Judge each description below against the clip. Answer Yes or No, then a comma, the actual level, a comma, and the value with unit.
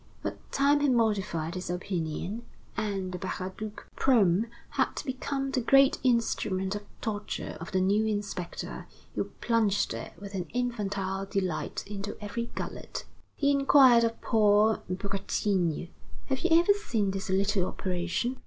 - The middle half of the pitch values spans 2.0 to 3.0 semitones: No, average, 4.0 semitones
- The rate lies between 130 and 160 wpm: Yes, average, 140 wpm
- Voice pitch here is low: No, high, 205 Hz